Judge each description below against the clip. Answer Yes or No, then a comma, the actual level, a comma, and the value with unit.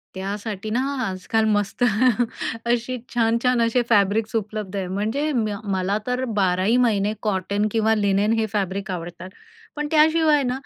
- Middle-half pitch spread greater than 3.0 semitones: Yes, average, 3.4 semitones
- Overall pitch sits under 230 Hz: Yes, high, 215 Hz